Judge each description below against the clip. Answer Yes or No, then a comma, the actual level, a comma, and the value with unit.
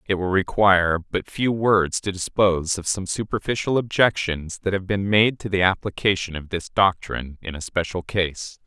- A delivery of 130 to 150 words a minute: No, average, 180 wpm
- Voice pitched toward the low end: Yes, very low, 95 Hz